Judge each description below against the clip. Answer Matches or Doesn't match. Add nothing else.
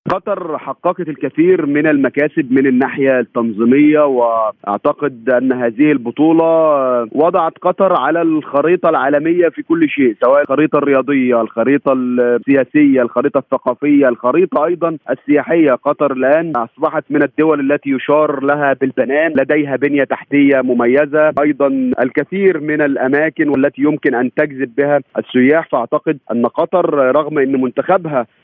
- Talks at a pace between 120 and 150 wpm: Matches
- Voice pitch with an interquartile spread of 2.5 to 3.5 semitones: Matches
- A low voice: Doesn't match